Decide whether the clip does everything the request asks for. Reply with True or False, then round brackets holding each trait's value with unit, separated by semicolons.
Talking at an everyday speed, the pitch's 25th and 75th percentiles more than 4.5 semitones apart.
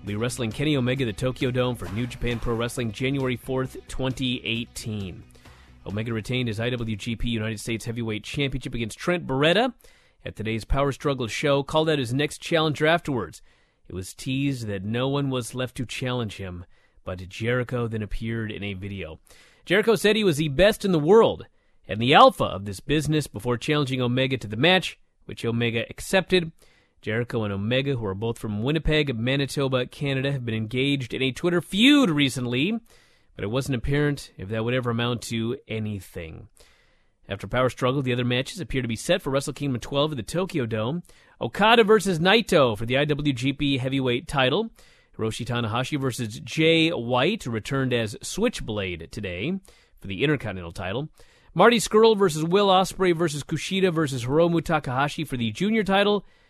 True (170 wpm; 5.2 semitones)